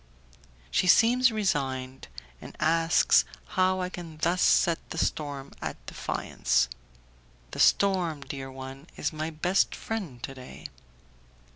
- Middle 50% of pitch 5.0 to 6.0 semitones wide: Yes, average, 5.3 semitones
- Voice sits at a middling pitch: Yes, medium, 160 Hz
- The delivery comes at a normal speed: No, slow, 125 wpm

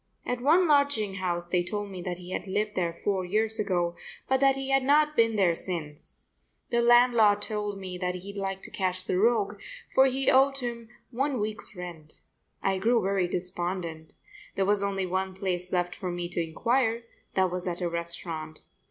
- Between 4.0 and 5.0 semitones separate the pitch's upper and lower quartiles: Yes, average, 4.5 semitones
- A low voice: No, high, 195 Hz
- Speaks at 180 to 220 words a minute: Yes, average, 190 wpm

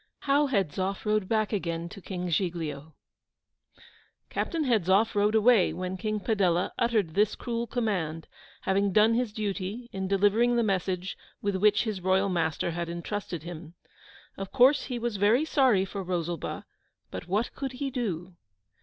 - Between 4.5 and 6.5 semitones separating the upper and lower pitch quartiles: No, average, 4.1 semitones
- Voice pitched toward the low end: No, high, 200 Hz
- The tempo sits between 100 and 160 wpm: Yes, average, 155 wpm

